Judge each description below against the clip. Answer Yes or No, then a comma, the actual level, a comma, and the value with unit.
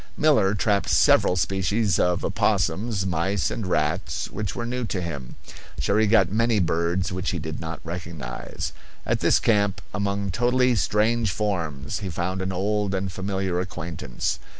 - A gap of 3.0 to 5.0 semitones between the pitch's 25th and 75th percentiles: Yes, average, 3.5 semitones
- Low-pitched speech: Yes, very low, 95 Hz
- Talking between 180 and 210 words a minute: No, average, 150 wpm